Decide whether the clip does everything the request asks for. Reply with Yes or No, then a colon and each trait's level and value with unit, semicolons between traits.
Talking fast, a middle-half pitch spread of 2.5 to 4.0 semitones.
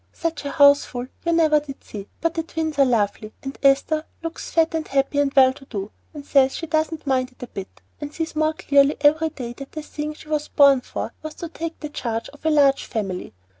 Yes: fast, 235 wpm; average, 3.0 semitones